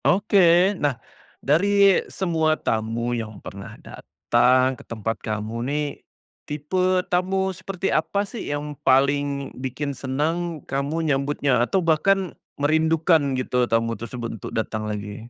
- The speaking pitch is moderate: Yes, medium, 145 Hz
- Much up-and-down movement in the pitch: Yes, wide, 6.2 semitones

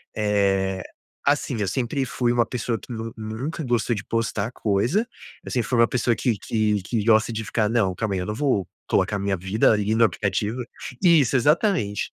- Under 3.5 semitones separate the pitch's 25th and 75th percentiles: Yes, average, 3.1 semitones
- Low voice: Yes, low, 110 Hz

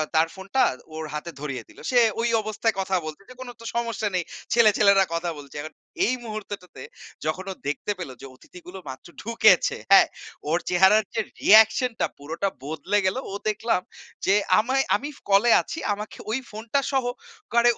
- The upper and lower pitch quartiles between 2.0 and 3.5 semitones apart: No, average, 5.1 semitones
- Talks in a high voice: Yes, high, 200 Hz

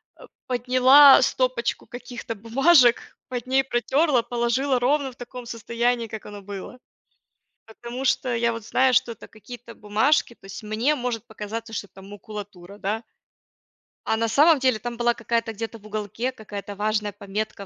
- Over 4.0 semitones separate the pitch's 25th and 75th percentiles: No, average, 2.9 semitones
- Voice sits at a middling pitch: No, high, 235 Hz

